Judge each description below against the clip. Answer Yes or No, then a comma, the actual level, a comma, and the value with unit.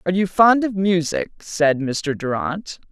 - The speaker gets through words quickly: No, average, 165 wpm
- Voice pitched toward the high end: No, medium, 180 Hz